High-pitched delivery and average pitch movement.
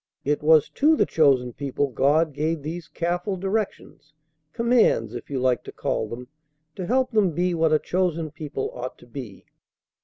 No: medium, 155 Hz; average, 4.9 semitones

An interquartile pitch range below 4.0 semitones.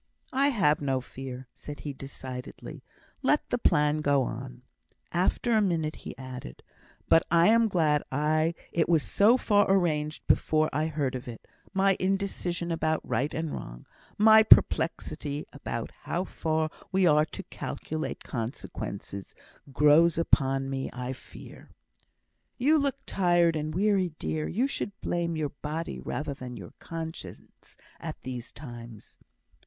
No: average, 4.5 semitones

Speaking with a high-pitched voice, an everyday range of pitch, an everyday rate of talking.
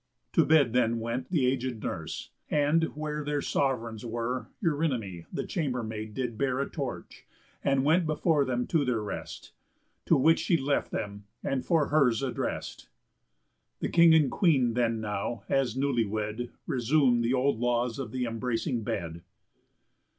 No: low, 125 Hz; average, 3.8 semitones; average, 155 wpm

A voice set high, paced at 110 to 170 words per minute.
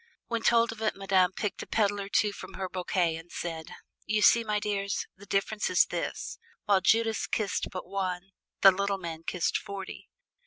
No: high, 195 Hz; average, 190 wpm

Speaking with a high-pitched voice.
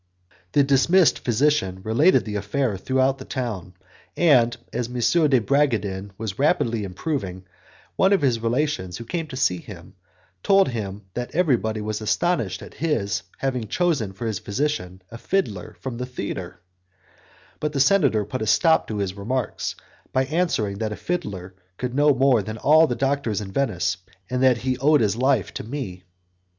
No: low, 120 Hz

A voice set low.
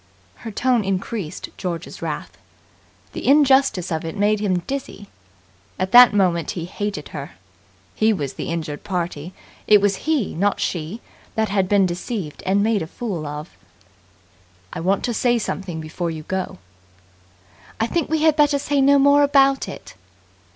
No: high, 200 Hz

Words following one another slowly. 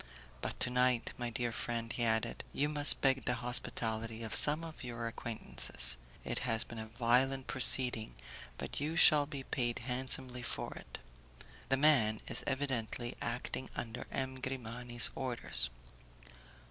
No: average, 150 wpm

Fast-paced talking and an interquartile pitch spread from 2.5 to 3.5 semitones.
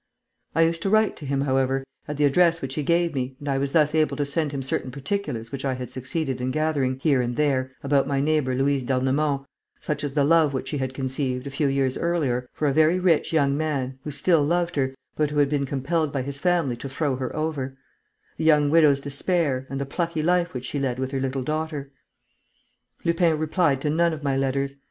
Yes: fast, 225 wpm; average, 2.9 semitones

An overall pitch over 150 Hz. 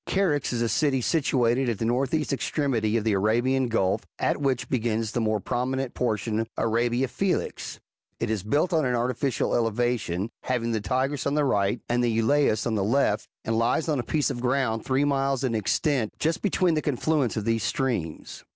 No: low, 120 Hz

